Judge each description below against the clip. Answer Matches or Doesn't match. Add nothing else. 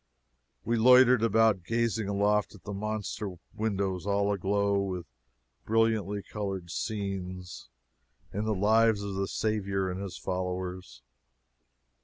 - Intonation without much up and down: Matches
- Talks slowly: Matches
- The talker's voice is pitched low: Matches